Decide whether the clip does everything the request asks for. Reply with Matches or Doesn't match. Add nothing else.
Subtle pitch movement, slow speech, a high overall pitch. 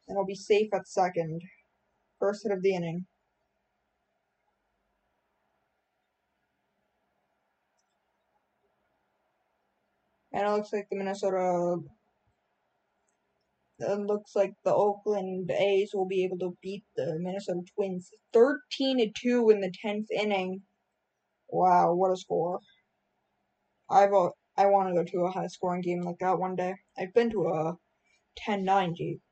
Matches